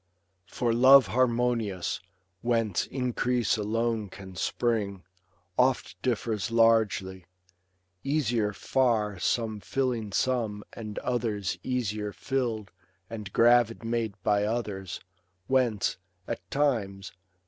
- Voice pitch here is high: No, low, 115 Hz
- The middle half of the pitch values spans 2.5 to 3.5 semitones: Yes, average, 2.9 semitones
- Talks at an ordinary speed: No, slow, 95 wpm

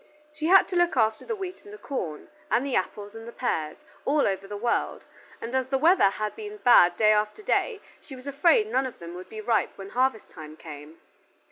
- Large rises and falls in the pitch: Yes, wide, 7.6 semitones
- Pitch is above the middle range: Yes, high, 240 Hz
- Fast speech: Yes, fast, 225 wpm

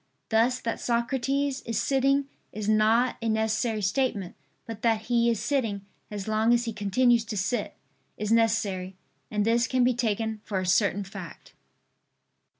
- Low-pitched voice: No, high, 225 Hz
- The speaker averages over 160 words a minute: No, average, 155 wpm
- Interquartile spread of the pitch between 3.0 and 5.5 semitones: No, narrow, 2.5 semitones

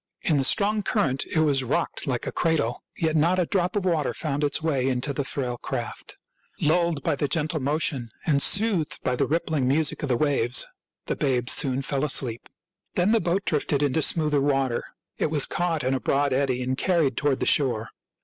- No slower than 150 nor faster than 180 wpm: No, fast, 205 wpm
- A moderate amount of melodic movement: Yes, average, 3.5 semitones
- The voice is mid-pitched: Yes, medium, 145 Hz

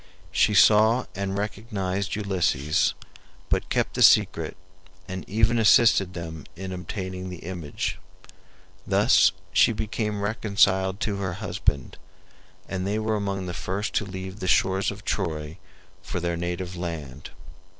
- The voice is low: Yes, very low, 95 Hz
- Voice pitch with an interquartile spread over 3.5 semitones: No, average, 2.7 semitones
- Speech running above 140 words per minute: No, slow, 135 wpm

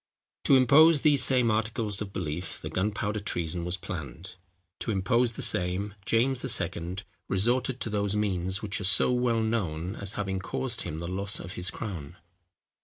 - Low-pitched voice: Yes, low, 100 Hz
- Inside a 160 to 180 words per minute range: Yes, average, 170 wpm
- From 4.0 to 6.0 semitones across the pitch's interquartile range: Yes, average, 4.3 semitones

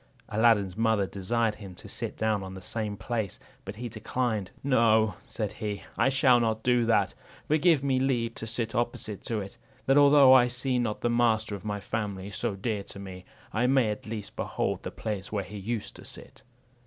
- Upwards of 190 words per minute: Yes, fast, 205 wpm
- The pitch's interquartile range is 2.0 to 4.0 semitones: Yes, average, 2.8 semitones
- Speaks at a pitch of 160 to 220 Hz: No, low, 110 Hz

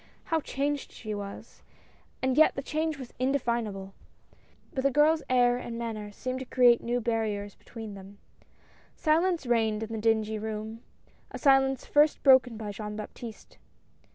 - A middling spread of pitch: Yes, average, 3.9 semitones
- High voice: Yes, high, 235 Hz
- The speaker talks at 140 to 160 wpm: Yes, average, 155 wpm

